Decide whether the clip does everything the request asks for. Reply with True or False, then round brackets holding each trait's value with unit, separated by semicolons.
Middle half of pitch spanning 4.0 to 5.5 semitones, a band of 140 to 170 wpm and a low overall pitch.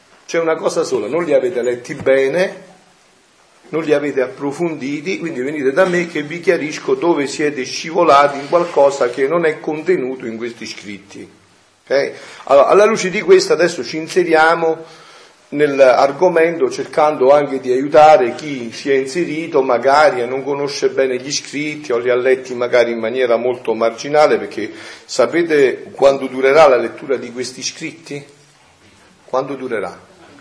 False (4.6 semitones; 150 wpm; 145 Hz)